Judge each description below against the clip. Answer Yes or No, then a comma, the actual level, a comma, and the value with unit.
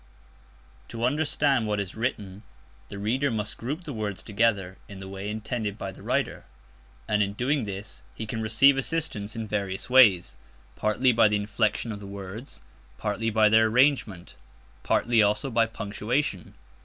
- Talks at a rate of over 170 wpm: No, average, 160 wpm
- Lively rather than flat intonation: No, average, 3.2 semitones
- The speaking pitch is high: No, low, 110 Hz